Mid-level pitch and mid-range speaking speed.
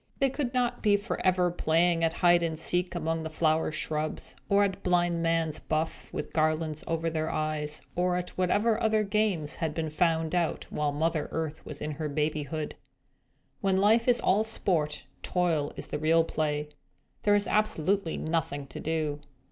Yes: medium, 165 Hz; average, 170 wpm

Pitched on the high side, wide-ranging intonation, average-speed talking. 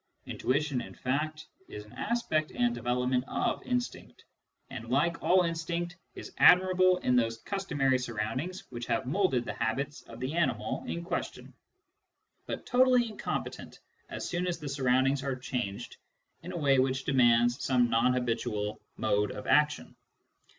No: low, 135 Hz; wide, 5.7 semitones; average, 150 wpm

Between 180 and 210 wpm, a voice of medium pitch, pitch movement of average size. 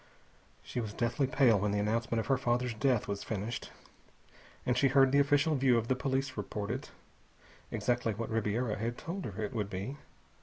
No: average, 190 wpm; low, 120 Hz; average, 3.8 semitones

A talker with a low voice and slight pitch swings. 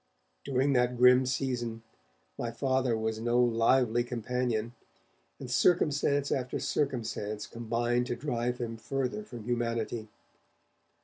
Yes: low, 120 Hz; narrow, 2.0 semitones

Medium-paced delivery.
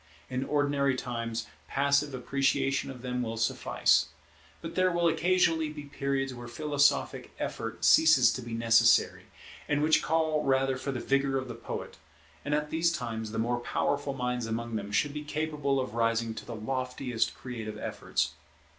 Yes: average, 165 wpm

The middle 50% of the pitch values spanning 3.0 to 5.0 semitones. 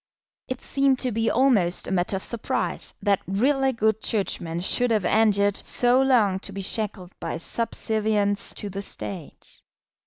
Yes: average, 3.7 semitones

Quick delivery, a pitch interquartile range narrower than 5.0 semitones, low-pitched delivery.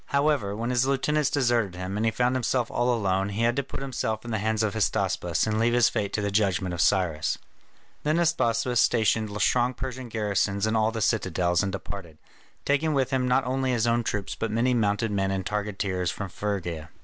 Yes: fast, 210 wpm; average, 4.0 semitones; low, 110 Hz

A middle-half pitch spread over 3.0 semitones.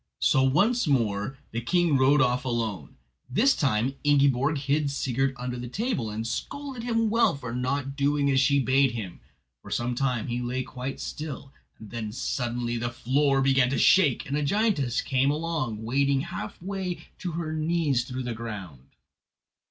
Yes: average, 3.6 semitones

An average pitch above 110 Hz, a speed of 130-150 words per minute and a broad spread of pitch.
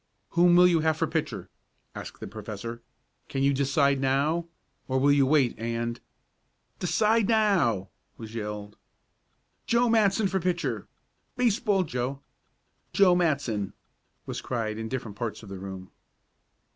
Yes: medium, 140 Hz; average, 140 wpm; wide, 7.9 semitones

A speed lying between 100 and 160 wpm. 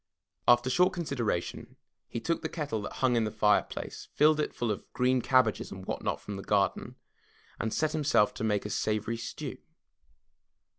No: average, 180 wpm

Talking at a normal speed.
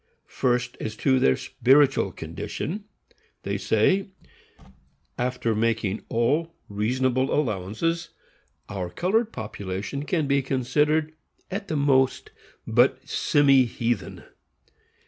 No: slow, 100 wpm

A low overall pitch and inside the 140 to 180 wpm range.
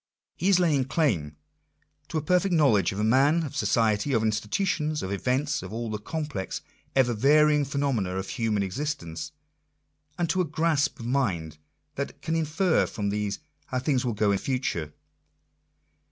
Yes: low, 130 Hz; average, 165 wpm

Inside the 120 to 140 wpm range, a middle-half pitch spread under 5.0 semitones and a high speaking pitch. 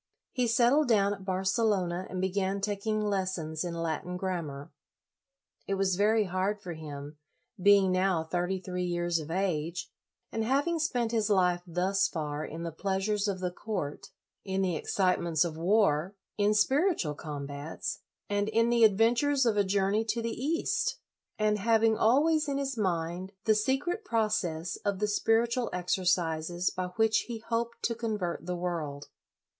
No: average, 160 wpm; average, 4.1 semitones; high, 195 Hz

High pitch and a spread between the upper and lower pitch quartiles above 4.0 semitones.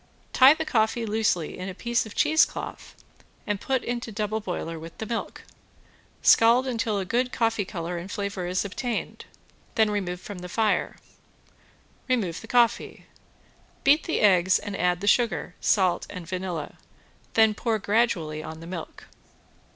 Yes: high, 205 Hz; average, 4.4 semitones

